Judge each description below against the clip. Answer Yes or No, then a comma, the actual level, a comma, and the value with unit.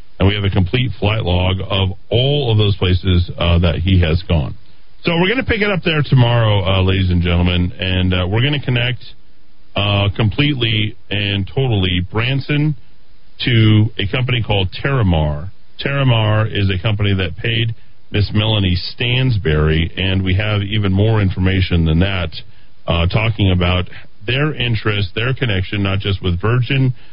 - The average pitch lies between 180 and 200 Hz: No, low, 100 Hz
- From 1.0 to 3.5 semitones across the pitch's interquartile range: No, average, 3.9 semitones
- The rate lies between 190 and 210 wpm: No, average, 165 wpm